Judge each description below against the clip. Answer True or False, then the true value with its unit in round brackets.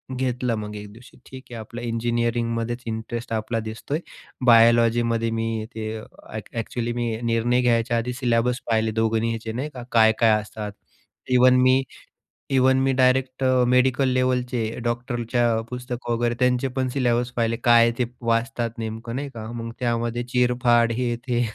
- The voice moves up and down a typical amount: False (1.5 semitones)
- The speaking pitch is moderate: False (120 Hz)